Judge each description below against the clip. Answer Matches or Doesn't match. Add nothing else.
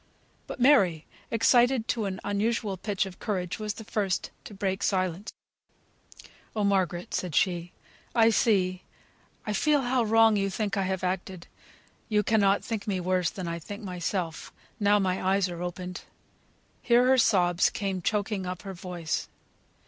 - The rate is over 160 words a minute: Doesn't match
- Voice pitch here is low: Doesn't match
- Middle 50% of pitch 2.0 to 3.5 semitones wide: Matches